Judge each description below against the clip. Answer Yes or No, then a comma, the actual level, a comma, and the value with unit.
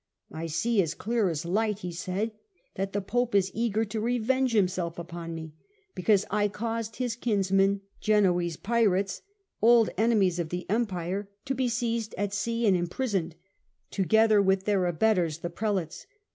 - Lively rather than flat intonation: No, average, 4.0 semitones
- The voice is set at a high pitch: Yes, high, 200 Hz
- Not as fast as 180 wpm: Yes, average, 170 wpm